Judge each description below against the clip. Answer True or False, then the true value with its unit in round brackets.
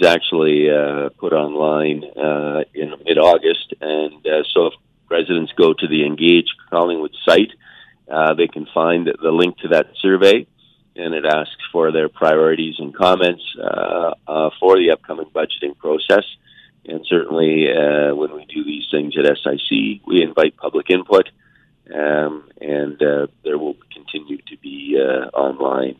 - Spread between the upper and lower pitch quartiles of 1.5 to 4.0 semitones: True (2.8 semitones)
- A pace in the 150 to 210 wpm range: True (155 wpm)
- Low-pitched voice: True (75 Hz)